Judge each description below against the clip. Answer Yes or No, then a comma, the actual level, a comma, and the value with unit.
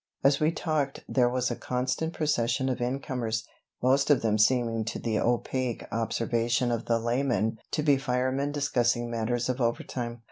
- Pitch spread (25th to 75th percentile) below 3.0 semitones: Yes, narrow, 2.5 semitones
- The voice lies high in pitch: No, low, 125 Hz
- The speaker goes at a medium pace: Yes, average, 170 wpm